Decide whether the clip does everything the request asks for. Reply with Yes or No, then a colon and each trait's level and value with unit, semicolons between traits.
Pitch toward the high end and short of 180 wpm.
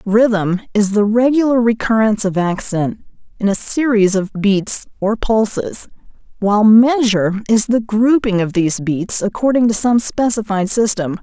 Yes: high, 215 Hz; average, 145 wpm